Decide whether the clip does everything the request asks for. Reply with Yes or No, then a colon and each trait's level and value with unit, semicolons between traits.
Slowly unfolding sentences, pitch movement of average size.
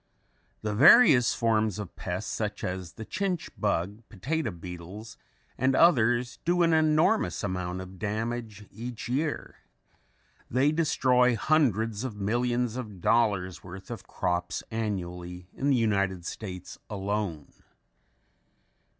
Yes: slow, 120 wpm; average, 4.9 semitones